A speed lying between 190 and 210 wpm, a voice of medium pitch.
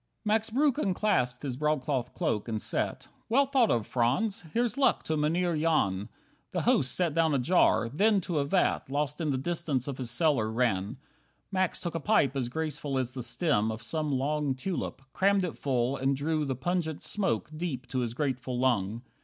Yes: average, 195 wpm; medium, 145 Hz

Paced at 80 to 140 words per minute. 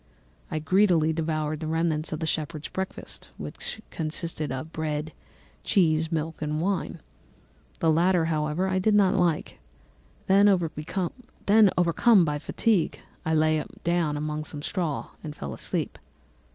Yes: slow, 135 wpm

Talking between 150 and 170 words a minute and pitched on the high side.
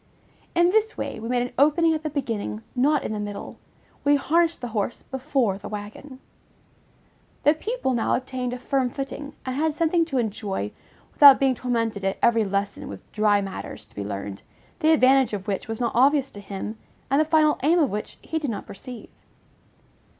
No: average, 190 wpm; very high, 255 Hz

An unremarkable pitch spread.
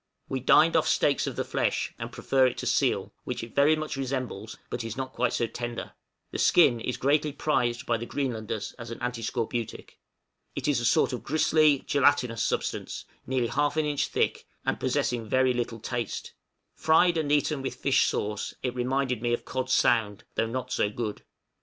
Yes: average, 3.1 semitones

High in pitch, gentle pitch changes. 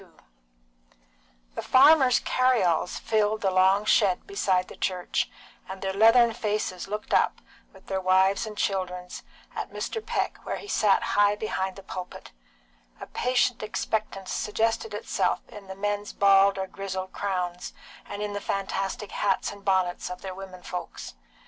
Yes: high, 195 Hz; narrow, 2.1 semitones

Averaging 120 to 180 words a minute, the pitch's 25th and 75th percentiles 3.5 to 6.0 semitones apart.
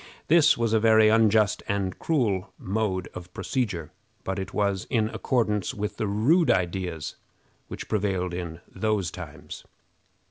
No: average, 140 wpm; average, 3.1 semitones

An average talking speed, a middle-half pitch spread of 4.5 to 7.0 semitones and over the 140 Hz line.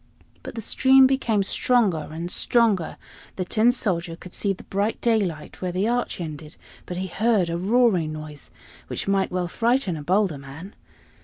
Yes: average, 170 wpm; average, 5.2 semitones; high, 190 Hz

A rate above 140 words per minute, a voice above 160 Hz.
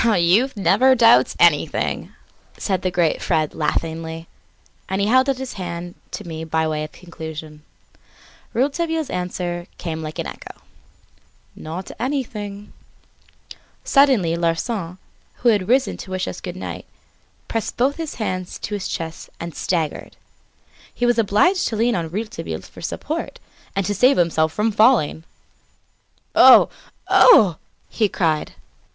No: slow, 135 wpm; high, 190 Hz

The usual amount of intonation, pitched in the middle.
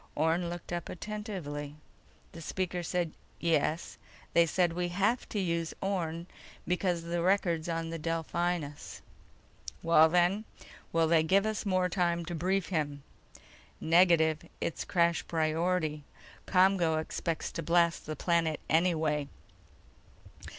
No: narrow, 2.0 semitones; medium, 170 Hz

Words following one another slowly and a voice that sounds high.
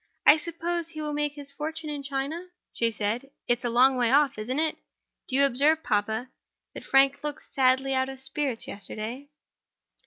No: average, 180 wpm; very high, 275 Hz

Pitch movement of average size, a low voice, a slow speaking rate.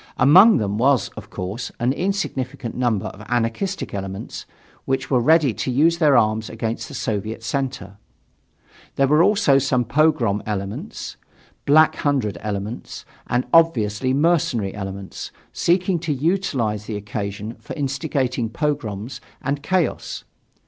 No: wide, 5.7 semitones; low, 125 Hz; slow, 130 wpm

